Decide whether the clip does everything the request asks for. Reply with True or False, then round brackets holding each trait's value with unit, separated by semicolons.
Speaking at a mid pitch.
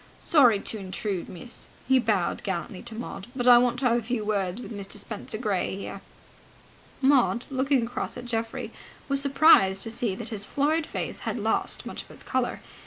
False (230 Hz)